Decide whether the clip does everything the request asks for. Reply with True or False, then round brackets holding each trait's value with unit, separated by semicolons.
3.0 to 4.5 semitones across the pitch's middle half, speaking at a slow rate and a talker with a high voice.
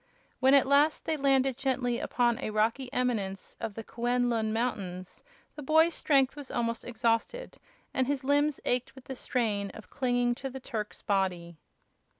False (3.4 semitones; 165 wpm; 245 Hz)